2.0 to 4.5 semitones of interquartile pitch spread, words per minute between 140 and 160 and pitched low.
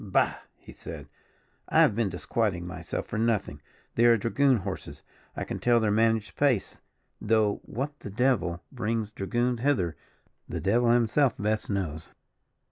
Yes: average, 3.3 semitones; average, 150 wpm; low, 110 Hz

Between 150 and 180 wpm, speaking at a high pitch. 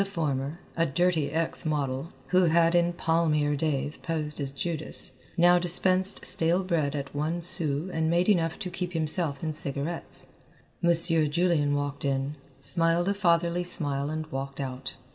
No: average, 160 wpm; medium, 160 Hz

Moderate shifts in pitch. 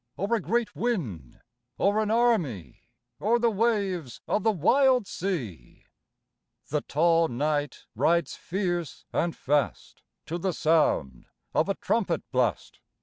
No: wide, 6.6 semitones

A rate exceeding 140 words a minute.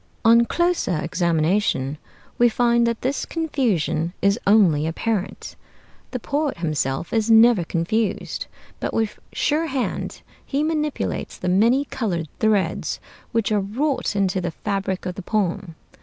No: slow, 135 wpm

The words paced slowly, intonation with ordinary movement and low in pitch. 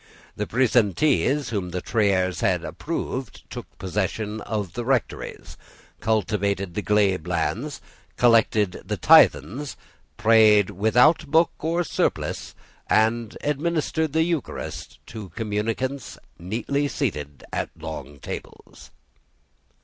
No: slow, 105 wpm; wide, 5.7 semitones; low, 110 Hz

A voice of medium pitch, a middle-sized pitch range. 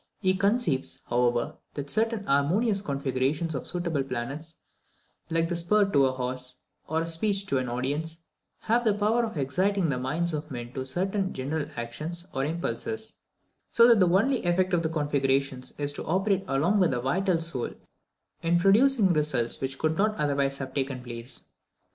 No: medium, 160 Hz; wide, 6.2 semitones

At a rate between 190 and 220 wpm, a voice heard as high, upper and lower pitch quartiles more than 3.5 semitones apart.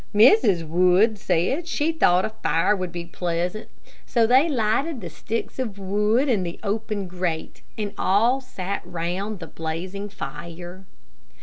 No: average, 150 wpm; high, 195 Hz; average, 4.1 semitones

